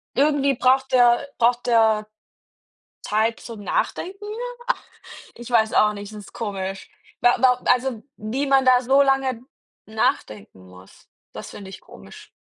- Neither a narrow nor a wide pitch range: Yes, average, 3.8 semitones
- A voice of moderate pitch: No, high, 240 Hz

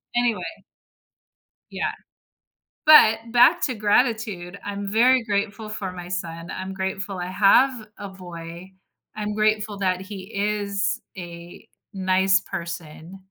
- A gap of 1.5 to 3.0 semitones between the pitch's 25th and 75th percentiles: Yes, average, 2.7 semitones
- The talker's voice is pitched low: No, high, 195 Hz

